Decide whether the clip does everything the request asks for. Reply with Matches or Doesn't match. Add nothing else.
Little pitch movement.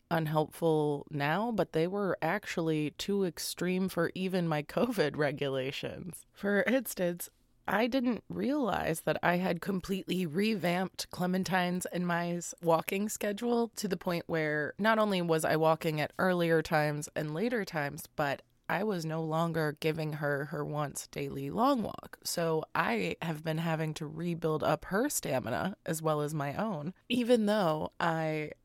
Doesn't match